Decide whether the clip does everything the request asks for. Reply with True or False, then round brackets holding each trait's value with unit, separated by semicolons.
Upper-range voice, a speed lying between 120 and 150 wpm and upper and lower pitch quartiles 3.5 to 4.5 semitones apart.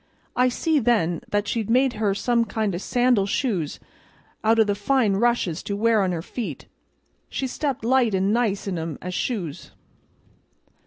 False (215 Hz; 170 wpm; 3.9 semitones)